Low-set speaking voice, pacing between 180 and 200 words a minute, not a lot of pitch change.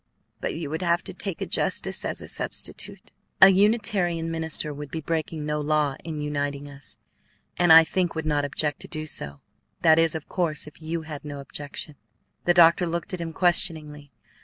No: medium, 160 Hz; average, 190 wpm; narrow, 2.3 semitones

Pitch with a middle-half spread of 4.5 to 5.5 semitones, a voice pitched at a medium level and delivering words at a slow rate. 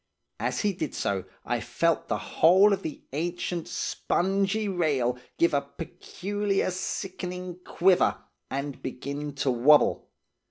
Yes: average, 5.0 semitones; medium, 175 Hz; slow, 125 wpm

